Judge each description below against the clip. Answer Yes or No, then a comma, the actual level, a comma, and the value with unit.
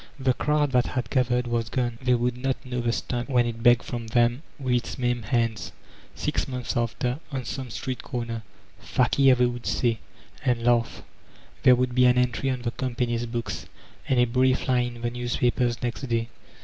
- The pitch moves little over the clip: Yes, narrow, 1.3 semitones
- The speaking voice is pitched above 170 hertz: No, low, 120 Hz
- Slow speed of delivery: No, average, 190 wpm